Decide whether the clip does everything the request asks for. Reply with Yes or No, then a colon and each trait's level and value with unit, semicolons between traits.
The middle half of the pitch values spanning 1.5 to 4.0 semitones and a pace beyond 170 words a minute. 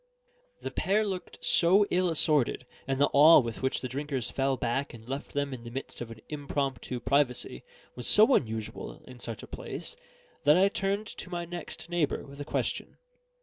No: wide, 5.6 semitones; average, 190 wpm